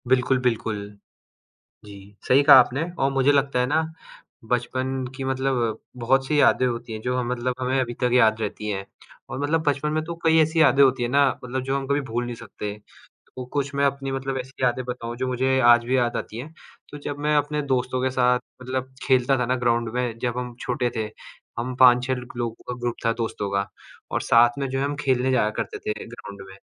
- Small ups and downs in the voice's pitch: Yes, narrow, 2.0 semitones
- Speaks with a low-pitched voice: Yes, low, 125 Hz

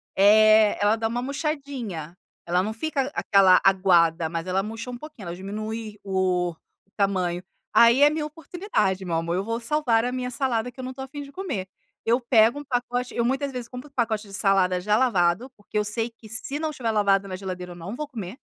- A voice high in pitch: Yes, high, 220 Hz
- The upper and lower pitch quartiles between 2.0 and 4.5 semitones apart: No, average, 5.0 semitones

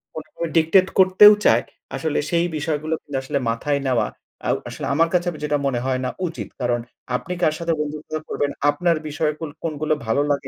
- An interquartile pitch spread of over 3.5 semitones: No, average, 2.8 semitones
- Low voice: No, medium, 150 Hz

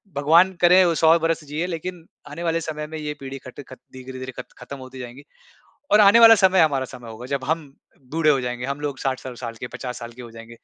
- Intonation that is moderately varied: Yes, average, 4.3 semitones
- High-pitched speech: No, medium, 140 Hz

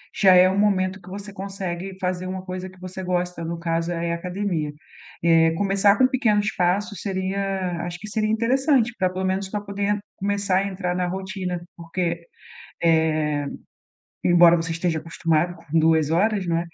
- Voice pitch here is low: No, medium, 185 Hz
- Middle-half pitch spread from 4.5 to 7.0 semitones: No, average, 2.7 semitones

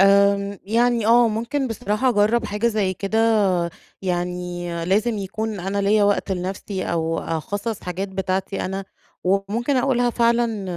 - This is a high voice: Yes, high, 200 Hz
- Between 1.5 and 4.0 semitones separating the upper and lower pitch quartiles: Yes, average, 3.2 semitones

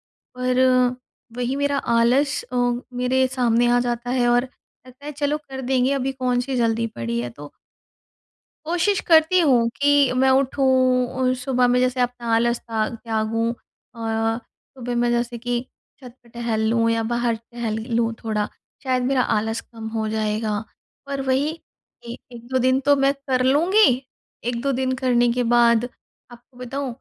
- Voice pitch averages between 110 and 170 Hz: No, high, 245 Hz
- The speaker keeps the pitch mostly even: Yes, narrow, 2.1 semitones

